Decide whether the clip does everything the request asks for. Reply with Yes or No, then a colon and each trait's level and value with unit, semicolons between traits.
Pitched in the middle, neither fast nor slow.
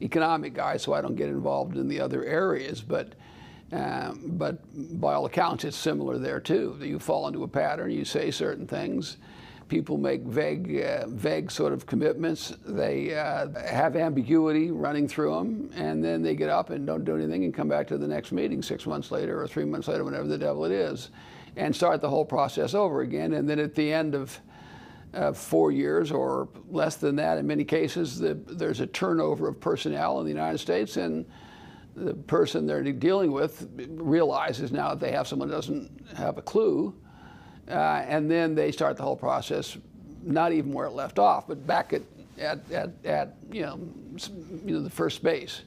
Yes: medium, 145 Hz; average, 195 wpm